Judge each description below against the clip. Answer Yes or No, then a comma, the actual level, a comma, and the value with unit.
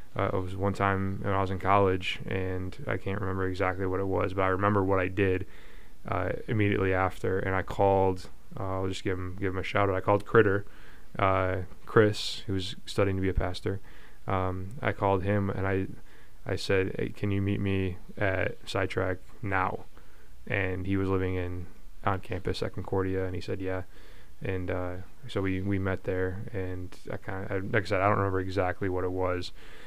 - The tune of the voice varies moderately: No, narrow, 1.1 semitones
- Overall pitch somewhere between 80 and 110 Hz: Yes, very low, 95 Hz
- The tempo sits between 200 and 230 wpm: Yes, fast, 205 wpm